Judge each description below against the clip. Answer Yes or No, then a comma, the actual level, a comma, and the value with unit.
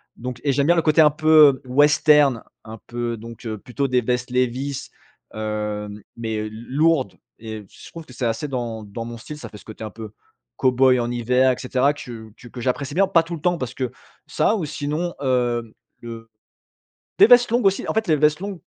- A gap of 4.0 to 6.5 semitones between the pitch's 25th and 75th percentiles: Yes, average, 4.4 semitones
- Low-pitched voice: Yes, low, 125 Hz